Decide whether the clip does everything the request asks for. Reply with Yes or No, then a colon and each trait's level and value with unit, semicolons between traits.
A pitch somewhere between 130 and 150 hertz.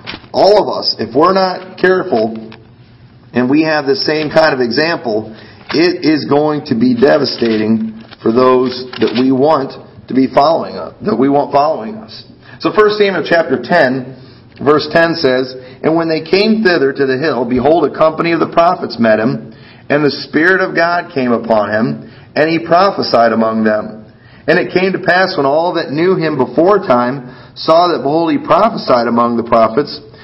Yes: medium, 140 Hz